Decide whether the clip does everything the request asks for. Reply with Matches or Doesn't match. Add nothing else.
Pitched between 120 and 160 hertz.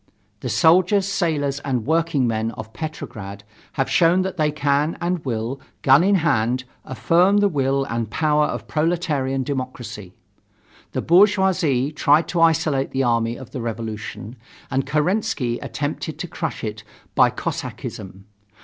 Matches